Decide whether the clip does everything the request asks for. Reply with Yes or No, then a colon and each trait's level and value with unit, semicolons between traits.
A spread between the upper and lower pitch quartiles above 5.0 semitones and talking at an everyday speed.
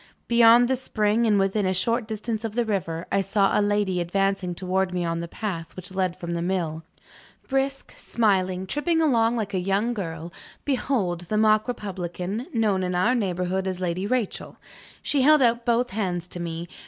No: average, 4.2 semitones; average, 185 wpm